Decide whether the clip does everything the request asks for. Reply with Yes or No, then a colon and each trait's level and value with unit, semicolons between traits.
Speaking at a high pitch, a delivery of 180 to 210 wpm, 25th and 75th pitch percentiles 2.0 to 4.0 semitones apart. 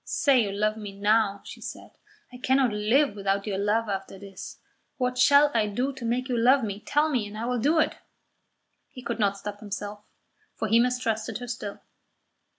Yes: high, 225 Hz; average, 195 wpm; average, 3.5 semitones